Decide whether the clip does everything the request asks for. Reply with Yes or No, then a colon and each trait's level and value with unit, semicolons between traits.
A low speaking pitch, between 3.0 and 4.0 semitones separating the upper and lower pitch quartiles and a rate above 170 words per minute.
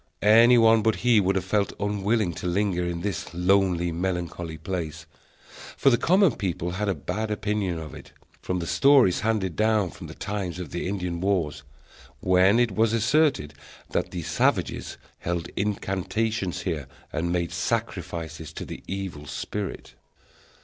No: very low, 95 Hz; average, 3.6 semitones; average, 155 wpm